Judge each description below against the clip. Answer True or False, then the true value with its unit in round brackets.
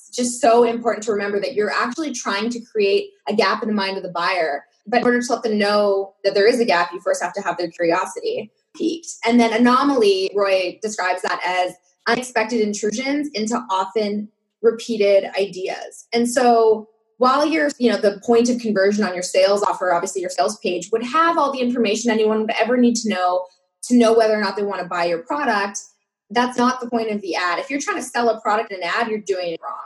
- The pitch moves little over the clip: False (3.7 semitones)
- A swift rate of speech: True (225 wpm)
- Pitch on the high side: True (220 Hz)